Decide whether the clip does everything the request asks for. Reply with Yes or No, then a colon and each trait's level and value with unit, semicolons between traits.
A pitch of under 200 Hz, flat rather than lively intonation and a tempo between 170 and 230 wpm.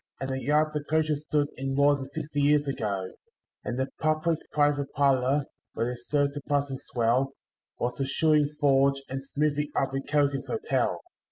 Yes: medium, 140 Hz; narrow, 1.7 semitones; average, 175 wpm